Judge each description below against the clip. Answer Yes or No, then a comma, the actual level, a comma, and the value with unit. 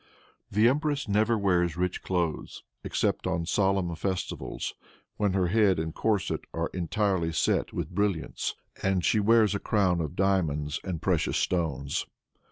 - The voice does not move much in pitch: No, average, 3.4 semitones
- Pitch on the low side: Yes, very low, 95 Hz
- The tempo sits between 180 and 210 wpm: No, average, 145 wpm